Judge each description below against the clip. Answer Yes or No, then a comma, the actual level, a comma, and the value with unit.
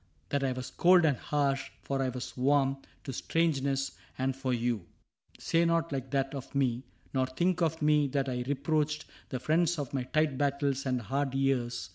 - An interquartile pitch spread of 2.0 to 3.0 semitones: Yes, narrow, 2.4 semitones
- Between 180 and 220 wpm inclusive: Yes, average, 190 wpm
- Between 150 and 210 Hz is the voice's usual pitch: No, low, 135 Hz